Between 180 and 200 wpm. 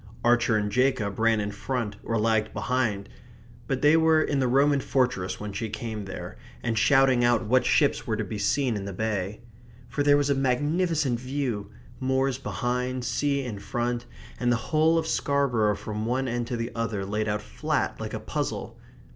Yes: average, 190 wpm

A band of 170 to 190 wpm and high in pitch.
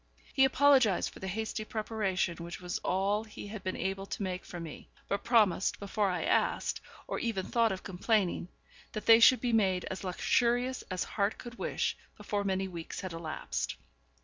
Yes: average, 180 wpm; high, 200 Hz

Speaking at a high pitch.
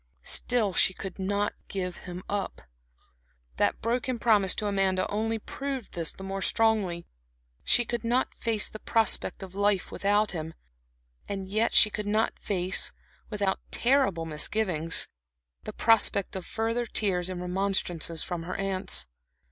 Yes: high, 200 Hz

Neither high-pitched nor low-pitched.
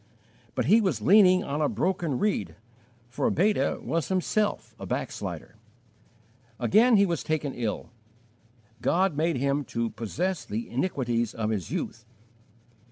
Yes: medium, 150 Hz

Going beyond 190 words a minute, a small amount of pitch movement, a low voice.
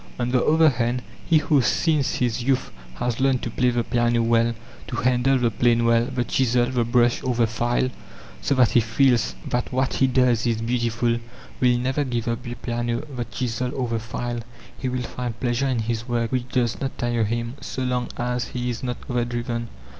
Yes: fast, 205 wpm; narrow, 1.4 semitones; low, 120 Hz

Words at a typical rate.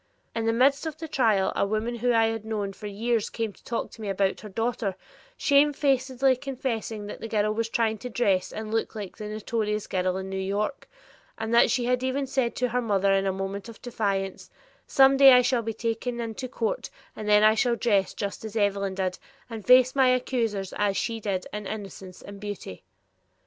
No: fast, 210 wpm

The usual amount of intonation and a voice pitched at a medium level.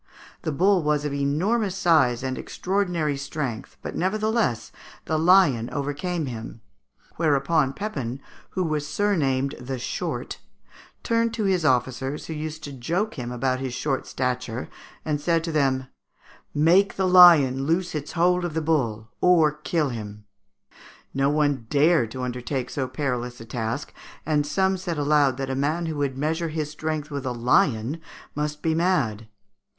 Yes: average, 4.3 semitones; medium, 150 Hz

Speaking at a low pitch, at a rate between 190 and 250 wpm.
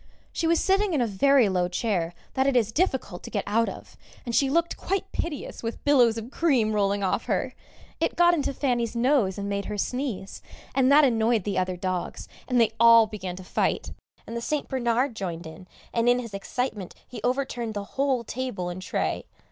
No: high, 235 Hz; fast, 205 wpm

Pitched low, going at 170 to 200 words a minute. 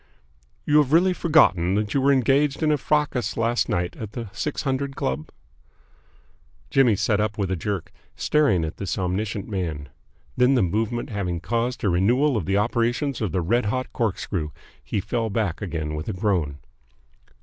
Yes: low, 110 Hz; average, 175 wpm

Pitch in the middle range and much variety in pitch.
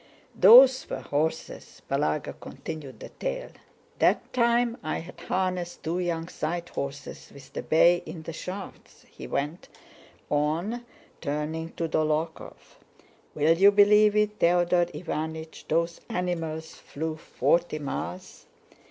No: medium, 170 Hz; average, 3.0 semitones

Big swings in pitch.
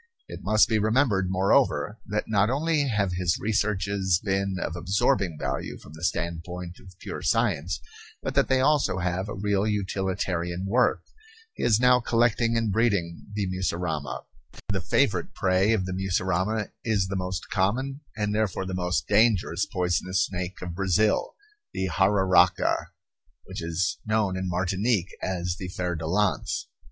No: average, 2.9 semitones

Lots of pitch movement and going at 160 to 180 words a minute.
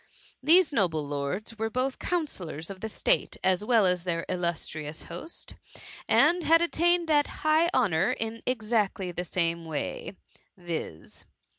No: wide, 8.5 semitones; average, 140 wpm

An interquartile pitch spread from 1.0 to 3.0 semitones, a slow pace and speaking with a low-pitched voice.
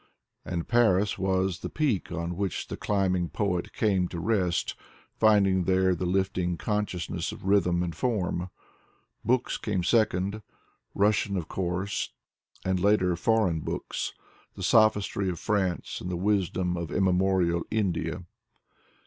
Yes: narrow, 2.6 semitones; slow, 130 wpm; very low, 95 Hz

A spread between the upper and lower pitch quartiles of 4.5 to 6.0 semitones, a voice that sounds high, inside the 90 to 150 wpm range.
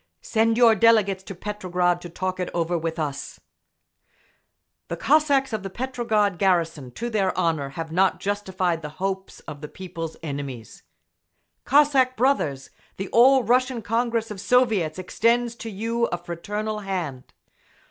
Yes: average, 5.3 semitones; high, 195 Hz; average, 145 wpm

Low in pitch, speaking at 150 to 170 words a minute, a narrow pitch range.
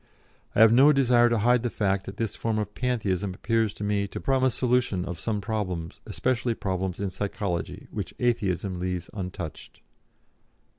No: low, 105 Hz; average, 165 wpm; average, 4.1 semitones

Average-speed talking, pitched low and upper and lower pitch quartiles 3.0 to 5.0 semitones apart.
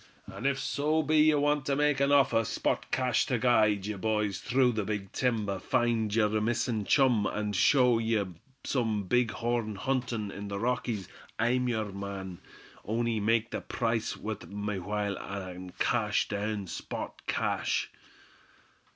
Yes: average, 155 wpm; low, 110 Hz; average, 3.3 semitones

